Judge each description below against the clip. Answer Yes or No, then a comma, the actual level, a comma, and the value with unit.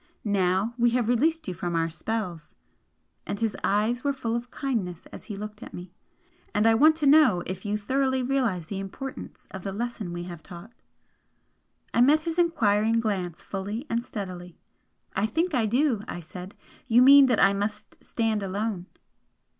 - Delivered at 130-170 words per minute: No, average, 180 wpm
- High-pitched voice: Yes, high, 215 Hz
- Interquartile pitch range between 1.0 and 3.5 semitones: No, average, 4.8 semitones